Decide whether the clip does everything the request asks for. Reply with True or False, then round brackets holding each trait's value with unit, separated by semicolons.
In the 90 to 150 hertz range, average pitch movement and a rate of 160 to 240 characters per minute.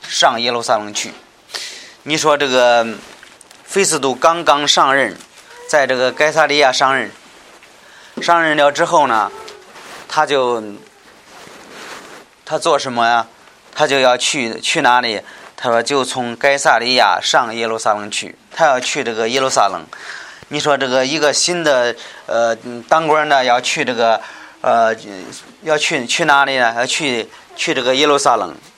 True (140 Hz; 4.2 semitones; 210 characters per minute)